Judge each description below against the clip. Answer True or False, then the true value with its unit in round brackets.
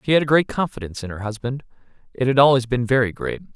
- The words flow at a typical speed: False (235 wpm)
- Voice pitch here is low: True (130 Hz)